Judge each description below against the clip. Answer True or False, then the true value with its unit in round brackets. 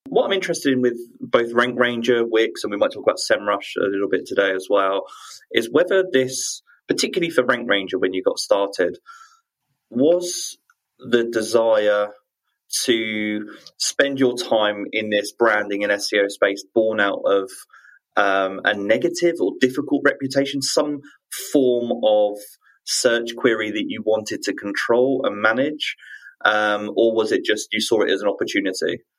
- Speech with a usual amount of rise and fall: False (8.0 semitones)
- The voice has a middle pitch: False (120 Hz)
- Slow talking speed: False (160 wpm)